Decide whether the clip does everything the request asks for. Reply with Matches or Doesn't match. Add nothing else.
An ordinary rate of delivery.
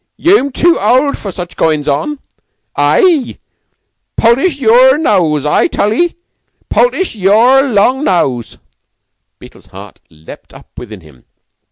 Doesn't match